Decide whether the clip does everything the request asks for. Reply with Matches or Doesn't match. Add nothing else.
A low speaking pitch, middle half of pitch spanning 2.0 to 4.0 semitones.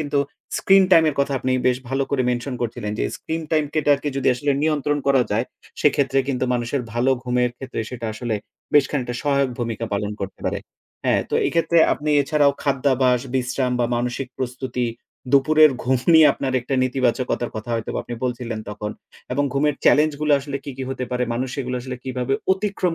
Matches